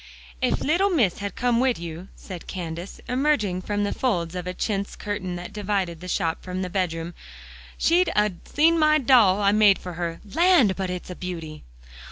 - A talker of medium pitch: No, high, 195 Hz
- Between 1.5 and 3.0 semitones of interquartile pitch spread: No, average, 5.0 semitones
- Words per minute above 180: Yes, average, 190 wpm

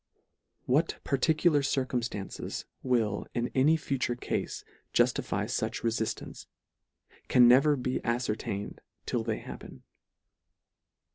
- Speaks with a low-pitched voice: Yes, low, 125 Hz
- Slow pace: Yes, slow, 95 wpm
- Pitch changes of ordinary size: Yes, average, 3.0 semitones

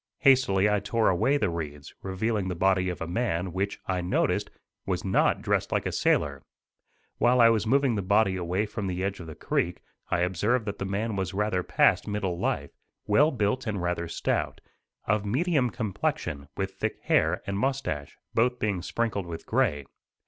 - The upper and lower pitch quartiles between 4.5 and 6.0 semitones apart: No, average, 4.1 semitones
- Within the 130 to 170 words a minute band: No, average, 185 wpm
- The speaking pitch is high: No, low, 100 Hz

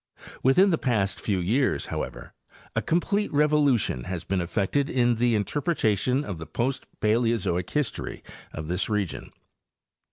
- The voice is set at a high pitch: No, low, 115 Hz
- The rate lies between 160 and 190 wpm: No, slow, 135 wpm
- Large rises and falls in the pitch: Yes, wide, 6.7 semitones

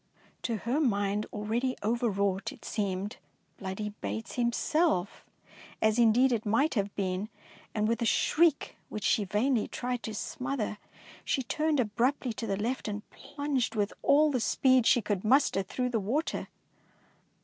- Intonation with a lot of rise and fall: No, average, 3.8 semitones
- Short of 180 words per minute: Yes, average, 155 wpm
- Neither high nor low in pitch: No, high, 225 Hz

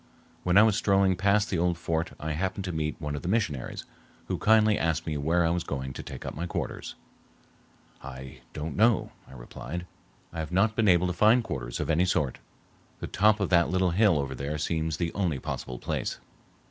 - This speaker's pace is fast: Yes, fast, 210 wpm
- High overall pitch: No, very low, 85 Hz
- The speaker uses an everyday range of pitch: Yes, average, 4.4 semitones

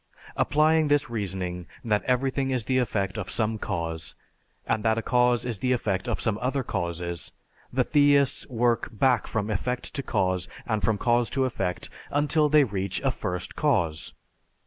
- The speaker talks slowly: No, average, 170 wpm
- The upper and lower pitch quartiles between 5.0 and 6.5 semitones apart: Yes, average, 5.3 semitones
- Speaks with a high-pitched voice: No, low, 115 Hz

